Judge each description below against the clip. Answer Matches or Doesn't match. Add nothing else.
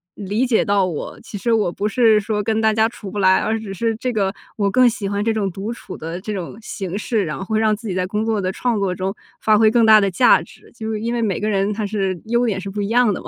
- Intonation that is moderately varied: Doesn't match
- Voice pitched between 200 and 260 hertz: Matches